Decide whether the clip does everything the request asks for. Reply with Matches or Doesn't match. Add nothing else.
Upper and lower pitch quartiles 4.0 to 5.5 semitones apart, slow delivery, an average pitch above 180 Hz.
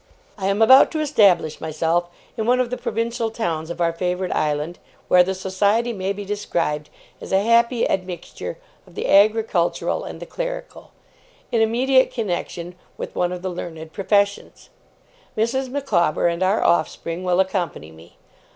Doesn't match